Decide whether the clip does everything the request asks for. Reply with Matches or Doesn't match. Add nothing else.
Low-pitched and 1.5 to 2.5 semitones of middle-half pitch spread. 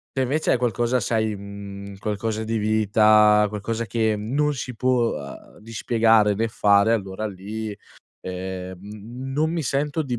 Doesn't match